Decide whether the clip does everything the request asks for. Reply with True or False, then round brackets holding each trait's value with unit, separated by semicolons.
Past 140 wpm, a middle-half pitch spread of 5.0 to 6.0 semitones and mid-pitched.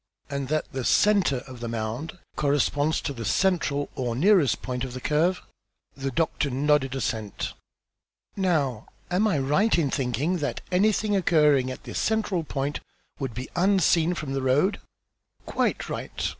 True (155 wpm; 5.3 semitones; 145 Hz)